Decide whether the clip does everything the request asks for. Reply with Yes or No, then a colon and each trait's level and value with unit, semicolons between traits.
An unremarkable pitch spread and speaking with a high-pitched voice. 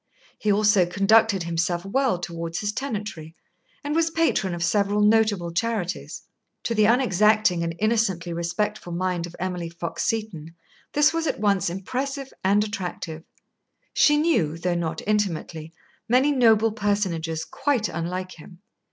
Yes: average, 4.4 semitones; high, 200 Hz